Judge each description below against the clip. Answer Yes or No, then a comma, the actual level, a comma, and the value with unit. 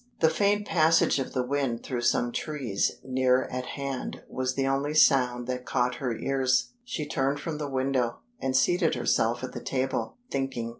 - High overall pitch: No, low, 135 Hz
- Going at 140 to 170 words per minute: No, average, 180 wpm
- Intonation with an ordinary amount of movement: No, narrow, 2.3 semitones